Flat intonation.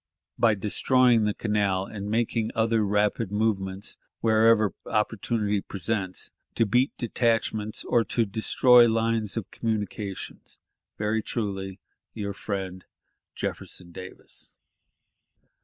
Yes: narrow, 2.3 semitones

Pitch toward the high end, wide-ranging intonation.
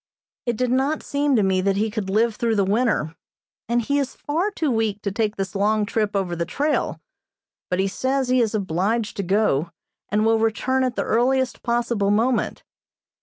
No: high, 220 Hz; average, 4.1 semitones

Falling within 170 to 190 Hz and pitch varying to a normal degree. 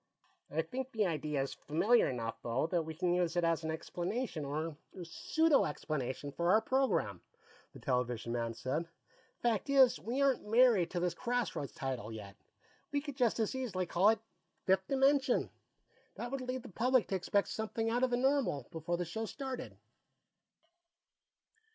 No: medium, 185 Hz; wide, 8.2 semitones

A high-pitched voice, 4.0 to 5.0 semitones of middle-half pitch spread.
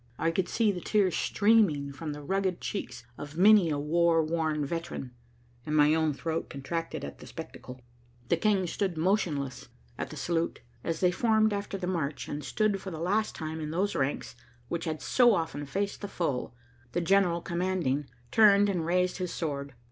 No: medium, 170 Hz; average, 4.4 semitones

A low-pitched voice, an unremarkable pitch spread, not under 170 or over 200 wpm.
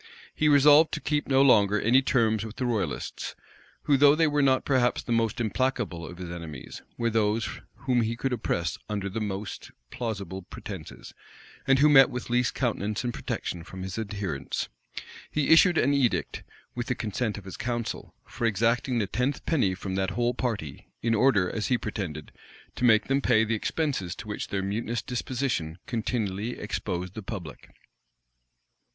Yes: low, 115 Hz; average, 4.5 semitones; average, 175 wpm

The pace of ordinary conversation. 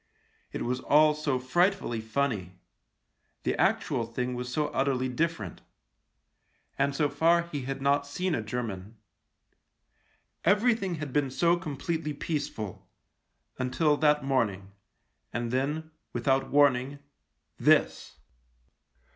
No: slow, 120 wpm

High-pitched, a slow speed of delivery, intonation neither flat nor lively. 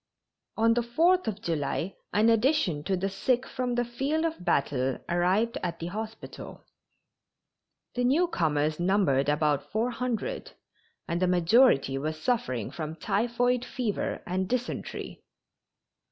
No: high, 205 Hz; slow, 130 wpm; wide, 6.9 semitones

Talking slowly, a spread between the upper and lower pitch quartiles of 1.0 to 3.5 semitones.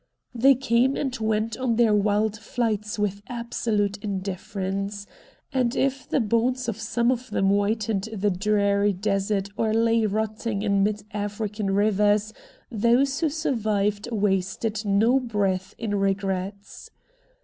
Yes: slow, 130 wpm; narrow, 2.4 semitones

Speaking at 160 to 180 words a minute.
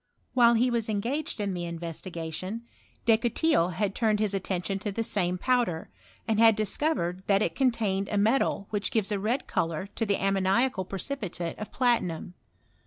Yes: average, 170 wpm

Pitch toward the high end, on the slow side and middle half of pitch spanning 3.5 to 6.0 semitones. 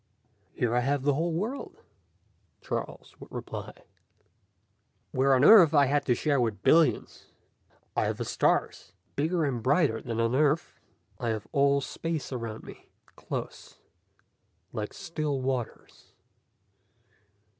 No: medium, 140 Hz; slow, 130 wpm; average, 4.2 semitones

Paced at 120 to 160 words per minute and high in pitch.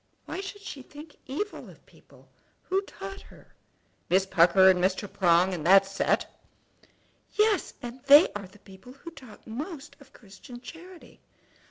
Yes: average, 155 wpm; very high, 250 Hz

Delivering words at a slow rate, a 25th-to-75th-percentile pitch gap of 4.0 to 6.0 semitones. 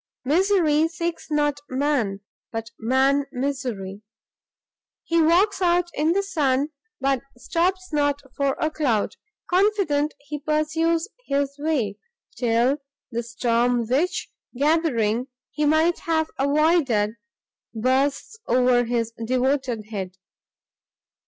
Yes: slow, 105 wpm; average, 4.7 semitones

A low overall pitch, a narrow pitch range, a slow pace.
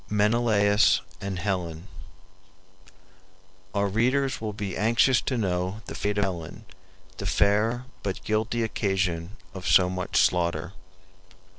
No: low, 100 Hz; average, 3.2 semitones; slow, 120 wpm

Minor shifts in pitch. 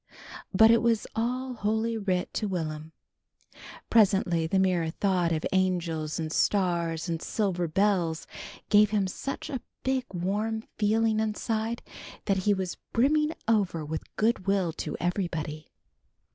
No: average, 4.5 semitones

